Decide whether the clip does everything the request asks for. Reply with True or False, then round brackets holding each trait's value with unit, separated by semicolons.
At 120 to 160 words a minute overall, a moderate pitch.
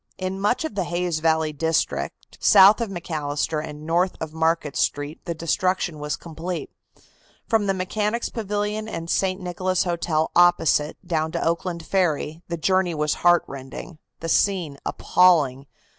True (145 wpm; 170 Hz)